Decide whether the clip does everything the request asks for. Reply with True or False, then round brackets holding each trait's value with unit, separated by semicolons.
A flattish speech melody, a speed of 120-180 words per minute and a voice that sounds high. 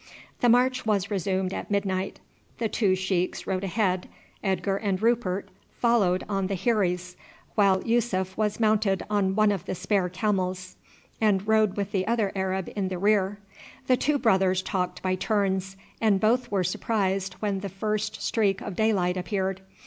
True (2.3 semitones; 165 wpm; 195 Hz)